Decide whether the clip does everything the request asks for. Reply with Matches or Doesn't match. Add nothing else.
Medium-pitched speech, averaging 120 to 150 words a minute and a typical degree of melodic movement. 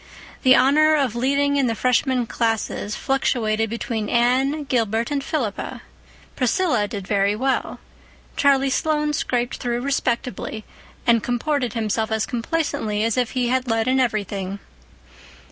Doesn't match